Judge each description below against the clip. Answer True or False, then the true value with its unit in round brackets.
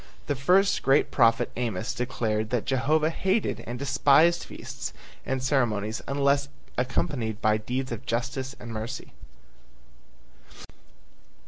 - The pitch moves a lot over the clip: False (3.3 semitones)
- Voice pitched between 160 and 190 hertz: False (130 Hz)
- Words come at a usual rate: False (115 wpm)